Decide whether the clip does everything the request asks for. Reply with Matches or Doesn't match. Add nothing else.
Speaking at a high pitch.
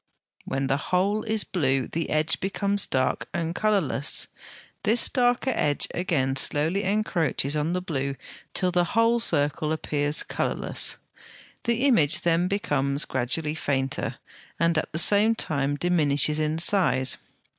Doesn't match